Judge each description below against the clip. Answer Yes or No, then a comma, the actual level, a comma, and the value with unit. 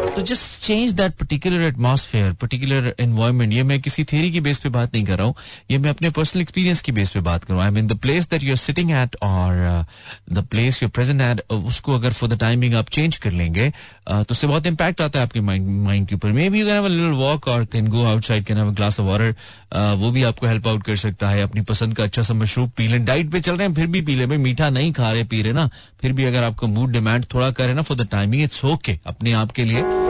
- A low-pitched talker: Yes, low, 120 Hz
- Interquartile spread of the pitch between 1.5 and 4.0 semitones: No, average, 5.2 semitones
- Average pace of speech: No, fast, 205 wpm